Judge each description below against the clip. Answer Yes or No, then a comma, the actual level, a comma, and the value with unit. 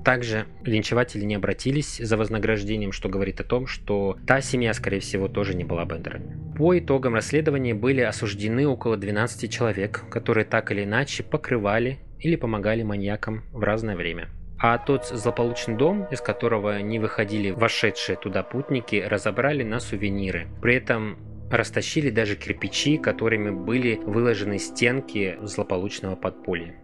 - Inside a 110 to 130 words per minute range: No, average, 140 wpm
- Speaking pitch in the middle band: No, low, 110 Hz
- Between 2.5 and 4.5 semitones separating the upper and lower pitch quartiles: Yes, average, 3.2 semitones